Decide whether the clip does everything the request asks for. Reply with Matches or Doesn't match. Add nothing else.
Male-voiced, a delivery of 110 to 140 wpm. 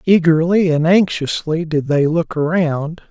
Matches